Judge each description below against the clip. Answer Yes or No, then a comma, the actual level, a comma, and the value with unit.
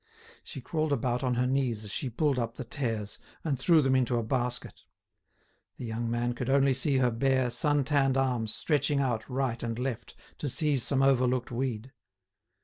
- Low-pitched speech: Yes, low, 130 Hz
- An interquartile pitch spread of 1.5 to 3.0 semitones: Yes, narrow, 2.4 semitones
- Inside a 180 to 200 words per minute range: Yes, average, 185 wpm